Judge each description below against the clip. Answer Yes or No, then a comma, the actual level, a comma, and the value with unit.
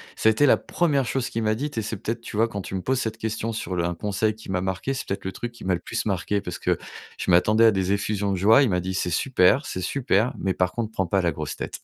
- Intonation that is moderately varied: Yes, average, 3.6 semitones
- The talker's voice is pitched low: Yes, low, 105 Hz